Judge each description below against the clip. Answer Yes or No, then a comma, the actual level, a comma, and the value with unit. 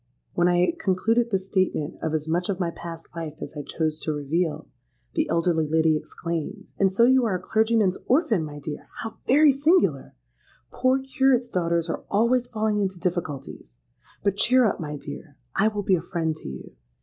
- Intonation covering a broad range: Yes, wide, 5.9 semitones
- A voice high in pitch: No, medium, 180 Hz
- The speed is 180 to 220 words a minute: Yes, average, 190 wpm